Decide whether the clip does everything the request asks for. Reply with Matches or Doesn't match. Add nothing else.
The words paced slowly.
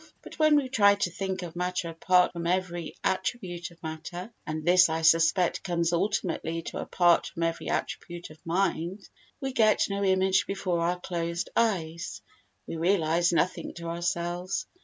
Doesn't match